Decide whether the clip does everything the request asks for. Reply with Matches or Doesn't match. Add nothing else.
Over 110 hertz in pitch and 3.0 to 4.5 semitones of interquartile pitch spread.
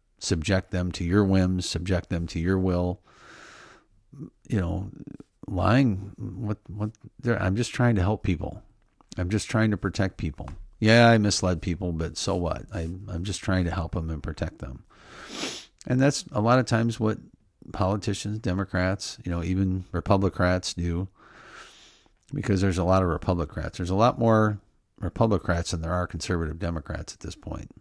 Doesn't match